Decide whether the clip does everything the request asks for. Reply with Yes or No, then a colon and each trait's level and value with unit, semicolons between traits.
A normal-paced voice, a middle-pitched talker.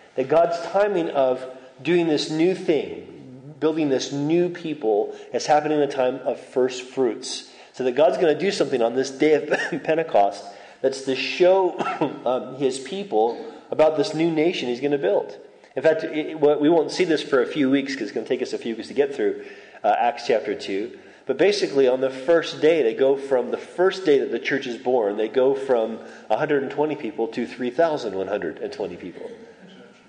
Yes: average, 195 wpm; medium, 155 Hz